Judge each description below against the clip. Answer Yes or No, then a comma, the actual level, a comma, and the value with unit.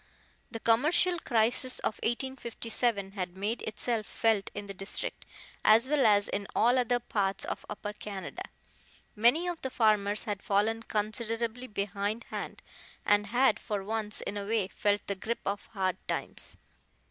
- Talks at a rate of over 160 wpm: No, average, 150 wpm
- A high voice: Yes, high, 215 Hz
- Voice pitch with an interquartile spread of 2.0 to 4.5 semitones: Yes, narrow, 2.6 semitones